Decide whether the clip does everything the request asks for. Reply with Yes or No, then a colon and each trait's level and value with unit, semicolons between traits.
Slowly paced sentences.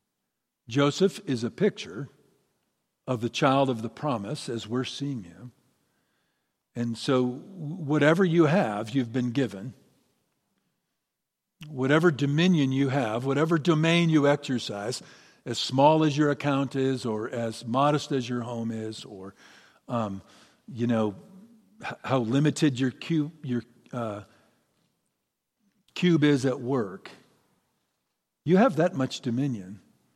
Yes: slow, 125 wpm